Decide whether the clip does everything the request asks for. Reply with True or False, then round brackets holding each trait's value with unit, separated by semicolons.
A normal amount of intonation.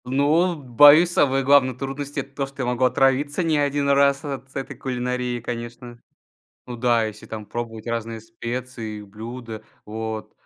True (3.1 semitones)